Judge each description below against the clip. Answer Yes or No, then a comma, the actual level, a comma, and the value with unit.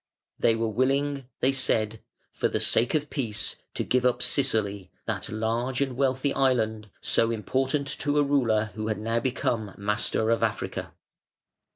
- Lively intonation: No, average, 3.5 semitones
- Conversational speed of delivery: Yes, average, 160 wpm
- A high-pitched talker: No, low, 120 Hz